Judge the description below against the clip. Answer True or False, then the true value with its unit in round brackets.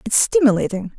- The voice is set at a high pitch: True (250 Hz)